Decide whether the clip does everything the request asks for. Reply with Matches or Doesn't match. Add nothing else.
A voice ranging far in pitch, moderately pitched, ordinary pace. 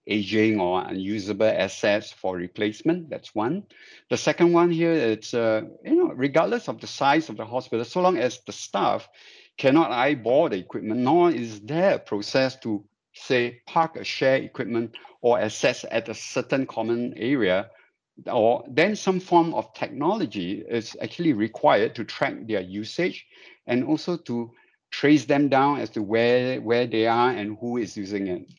Doesn't match